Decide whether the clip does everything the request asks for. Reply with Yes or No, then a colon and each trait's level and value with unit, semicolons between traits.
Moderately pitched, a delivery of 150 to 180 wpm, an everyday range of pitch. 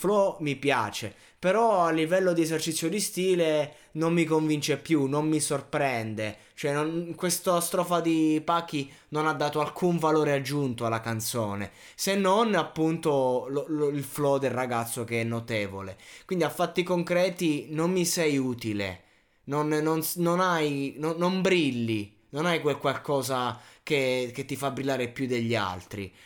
Yes: medium, 150 Hz; average, 160 wpm; average, 4.8 semitones